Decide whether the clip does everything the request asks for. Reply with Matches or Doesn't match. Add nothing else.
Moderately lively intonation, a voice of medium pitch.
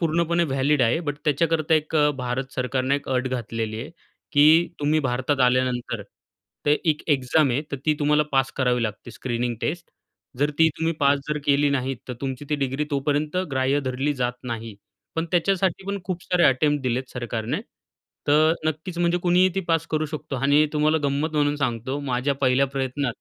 Matches